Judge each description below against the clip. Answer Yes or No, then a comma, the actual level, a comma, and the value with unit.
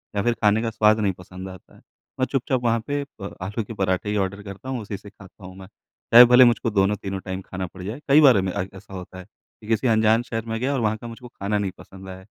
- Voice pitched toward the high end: No, low, 105 Hz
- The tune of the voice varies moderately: Yes, average, 3.5 semitones